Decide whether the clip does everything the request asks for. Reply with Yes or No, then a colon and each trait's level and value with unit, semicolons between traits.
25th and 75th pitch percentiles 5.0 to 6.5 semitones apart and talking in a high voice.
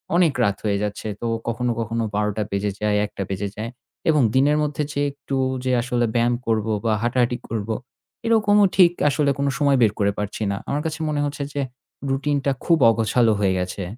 No: average, 5.3 semitones; low, 120 Hz